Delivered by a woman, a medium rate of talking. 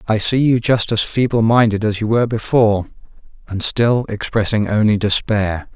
No: male; average, 165 wpm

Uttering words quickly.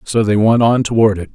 Yes: fast, 265 wpm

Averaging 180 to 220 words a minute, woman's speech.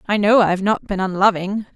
Yes: fast, 205 wpm; female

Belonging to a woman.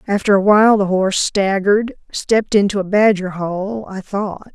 Yes: female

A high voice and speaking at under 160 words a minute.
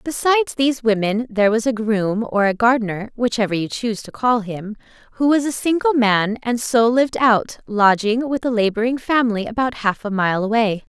No: high, 230 Hz; average, 190 wpm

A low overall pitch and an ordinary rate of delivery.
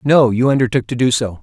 No: low, 125 Hz; fast, 210 wpm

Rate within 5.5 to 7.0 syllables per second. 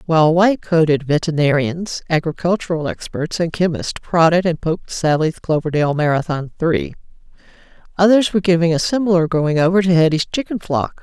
Yes: 5.7 syllables/s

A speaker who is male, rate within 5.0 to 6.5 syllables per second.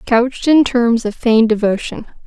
No: female; 5.1 syllables/s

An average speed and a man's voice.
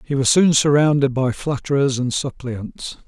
Yes: average, 155 wpm; male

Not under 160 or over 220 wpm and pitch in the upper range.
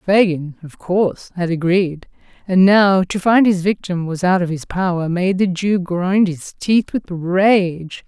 No: average, 180 wpm; medium, 180 Hz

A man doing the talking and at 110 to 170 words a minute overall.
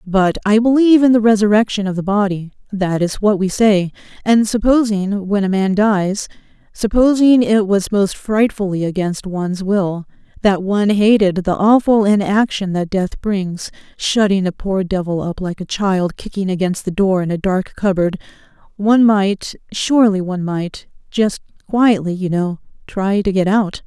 No: female; average, 160 wpm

